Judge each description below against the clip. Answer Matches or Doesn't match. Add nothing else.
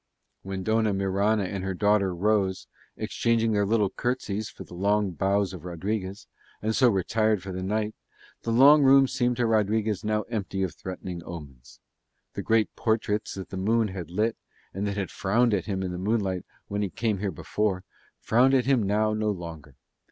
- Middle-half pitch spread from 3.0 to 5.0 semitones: Doesn't match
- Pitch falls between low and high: Doesn't match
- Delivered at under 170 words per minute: Doesn't match